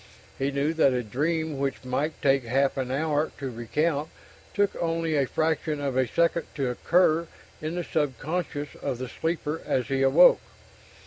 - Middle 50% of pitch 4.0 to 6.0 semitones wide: No, average, 3.2 semitones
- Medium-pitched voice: Yes, medium, 145 Hz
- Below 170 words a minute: No, average, 175 wpm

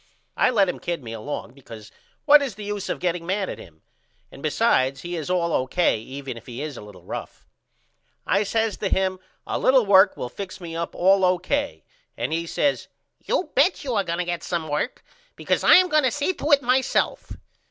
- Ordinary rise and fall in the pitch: No, wide, 7.2 semitones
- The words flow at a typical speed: No, fast, 215 wpm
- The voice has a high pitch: No, medium, 180 Hz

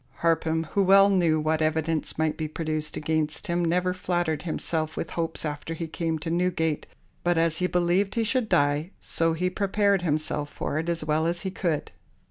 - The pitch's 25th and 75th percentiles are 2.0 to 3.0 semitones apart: Yes, narrow, 2.4 semitones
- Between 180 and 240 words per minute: Yes, average, 190 wpm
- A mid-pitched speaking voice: Yes, medium, 165 Hz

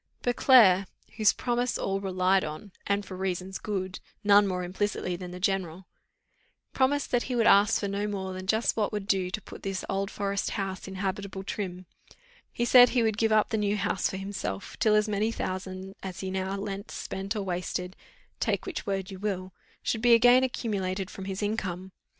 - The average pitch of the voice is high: Yes, high, 195 Hz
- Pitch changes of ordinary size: No, narrow, 2.2 semitones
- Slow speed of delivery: No, average, 195 wpm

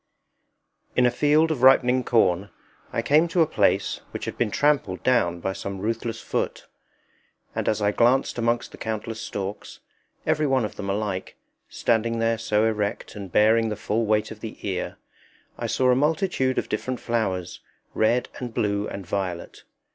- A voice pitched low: Yes, low, 115 Hz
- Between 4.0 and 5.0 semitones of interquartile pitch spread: No, average, 3.6 semitones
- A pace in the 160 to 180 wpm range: Yes, average, 170 wpm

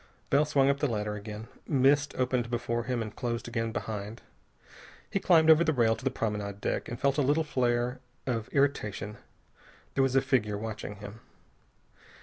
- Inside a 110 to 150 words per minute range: No, average, 175 wpm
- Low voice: Yes, low, 120 Hz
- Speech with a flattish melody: No, average, 4.2 semitones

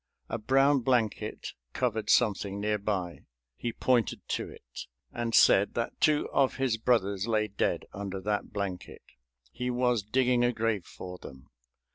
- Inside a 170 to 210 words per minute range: No, average, 150 wpm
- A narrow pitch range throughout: No, average, 3.6 semitones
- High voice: No, low, 110 Hz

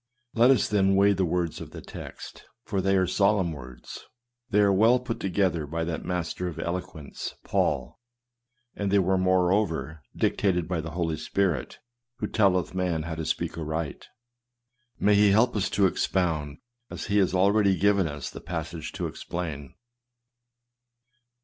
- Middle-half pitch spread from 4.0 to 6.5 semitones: No, average, 3.3 semitones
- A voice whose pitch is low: Yes, very low, 90 Hz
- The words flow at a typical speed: Yes, average, 160 wpm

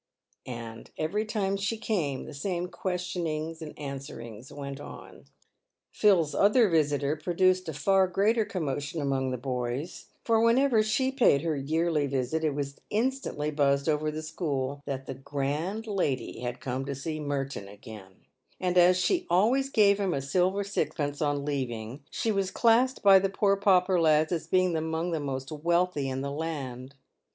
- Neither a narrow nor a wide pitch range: No, wide, 5.7 semitones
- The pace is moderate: Yes, average, 165 wpm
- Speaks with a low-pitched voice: No, medium, 155 Hz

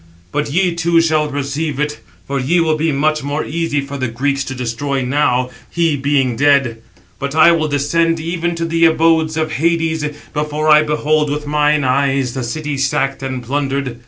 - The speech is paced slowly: No, average, 185 wpm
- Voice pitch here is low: No, medium, 150 Hz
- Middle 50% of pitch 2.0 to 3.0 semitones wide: Yes, narrow, 2.6 semitones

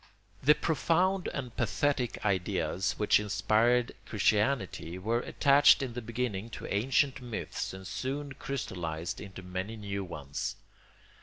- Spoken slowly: Yes, slow, 130 wpm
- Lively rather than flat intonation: Yes, wide, 5.7 semitones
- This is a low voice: Yes, low, 110 Hz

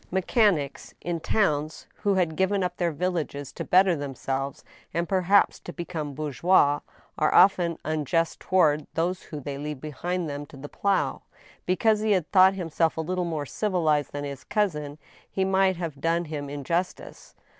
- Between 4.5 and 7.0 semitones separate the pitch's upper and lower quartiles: No, average, 4.0 semitones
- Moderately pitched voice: Yes, medium, 165 Hz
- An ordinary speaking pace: Yes, average, 170 wpm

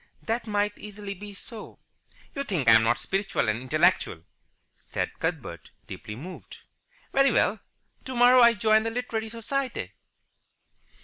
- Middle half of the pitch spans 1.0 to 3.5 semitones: No, average, 4.7 semitones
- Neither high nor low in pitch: No, high, 210 Hz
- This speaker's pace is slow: Yes, slow, 130 wpm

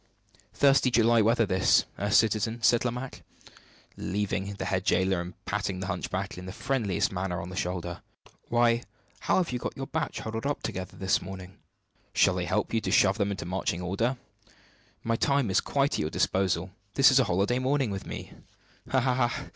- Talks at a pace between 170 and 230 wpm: Yes, average, 190 wpm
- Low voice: Yes, low, 105 Hz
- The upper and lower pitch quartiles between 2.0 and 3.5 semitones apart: No, average, 4.6 semitones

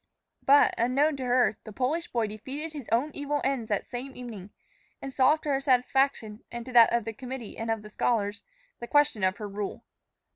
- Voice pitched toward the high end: Yes, high, 245 Hz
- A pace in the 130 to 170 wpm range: No, average, 195 wpm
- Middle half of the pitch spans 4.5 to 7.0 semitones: No, average, 3.7 semitones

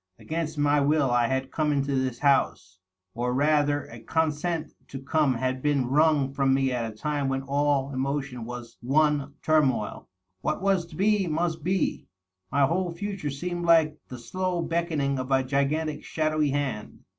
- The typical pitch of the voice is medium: Yes, medium, 145 Hz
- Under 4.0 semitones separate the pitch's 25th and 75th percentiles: Yes, average, 3.0 semitones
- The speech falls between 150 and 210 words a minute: Yes, average, 170 wpm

